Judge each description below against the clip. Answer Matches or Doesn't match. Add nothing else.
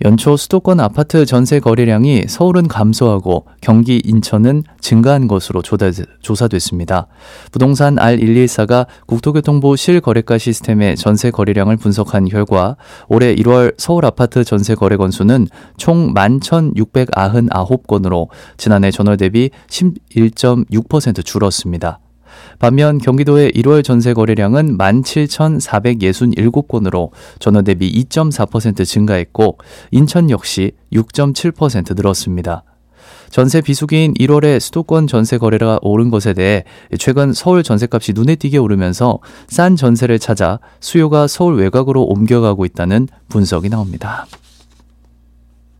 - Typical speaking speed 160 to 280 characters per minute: Matches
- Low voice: Matches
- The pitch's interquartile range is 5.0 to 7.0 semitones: Matches